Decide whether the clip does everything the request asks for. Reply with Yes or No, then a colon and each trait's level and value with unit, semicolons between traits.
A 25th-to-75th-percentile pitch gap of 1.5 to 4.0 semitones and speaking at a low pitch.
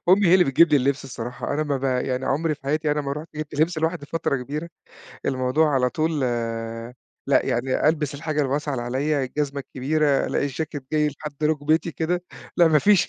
No: average, 3.0 semitones; medium, 145 Hz